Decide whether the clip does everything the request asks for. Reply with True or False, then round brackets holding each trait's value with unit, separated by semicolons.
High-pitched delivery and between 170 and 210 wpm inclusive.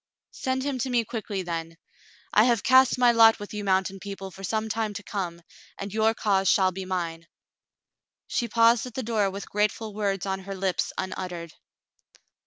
True (205 Hz; 185 wpm)